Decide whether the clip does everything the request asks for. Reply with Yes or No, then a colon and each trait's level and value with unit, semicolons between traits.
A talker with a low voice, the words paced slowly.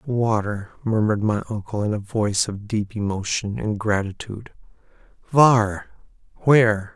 Yes: low, 105 Hz; slow, 120 wpm